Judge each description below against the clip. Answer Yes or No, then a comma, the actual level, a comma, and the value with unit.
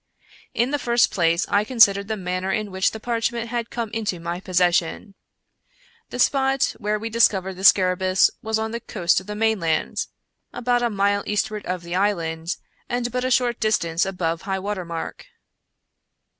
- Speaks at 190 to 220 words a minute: No, average, 170 wpm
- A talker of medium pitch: No, high, 205 Hz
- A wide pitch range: No, average, 3.9 semitones